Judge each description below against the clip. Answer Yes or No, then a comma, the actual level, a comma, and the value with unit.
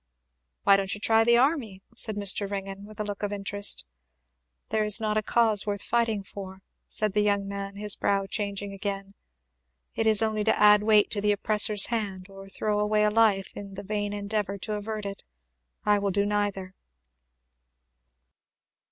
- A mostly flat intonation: Yes, narrow, 1.3 semitones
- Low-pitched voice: No, high, 205 Hz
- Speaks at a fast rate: No, average, 175 wpm